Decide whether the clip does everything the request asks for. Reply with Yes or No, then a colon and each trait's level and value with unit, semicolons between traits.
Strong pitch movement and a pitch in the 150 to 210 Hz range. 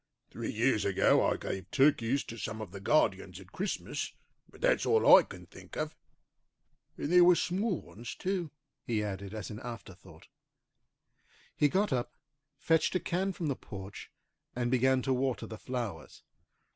No: wide, 7.4 semitones; low, 125 Hz